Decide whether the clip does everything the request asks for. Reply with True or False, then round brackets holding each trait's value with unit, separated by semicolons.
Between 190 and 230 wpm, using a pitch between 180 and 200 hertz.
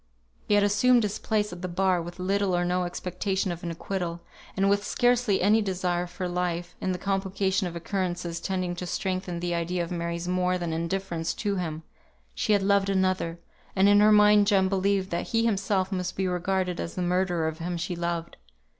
True (200 wpm; 185 Hz)